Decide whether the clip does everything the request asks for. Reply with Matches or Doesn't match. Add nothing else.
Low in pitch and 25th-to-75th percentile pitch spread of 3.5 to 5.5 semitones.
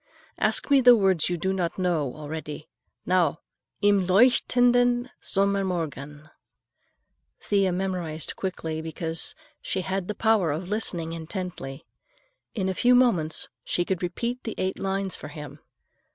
Doesn't match